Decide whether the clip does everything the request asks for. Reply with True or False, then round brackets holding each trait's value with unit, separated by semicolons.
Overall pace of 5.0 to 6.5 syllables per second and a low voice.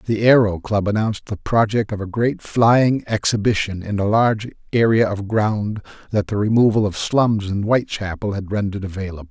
True (5.3 syllables/s; 105 Hz)